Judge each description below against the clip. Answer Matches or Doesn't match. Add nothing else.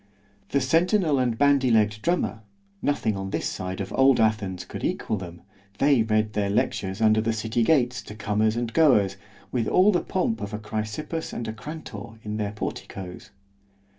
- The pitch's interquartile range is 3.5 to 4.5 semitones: Matches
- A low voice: Matches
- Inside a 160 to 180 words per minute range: Matches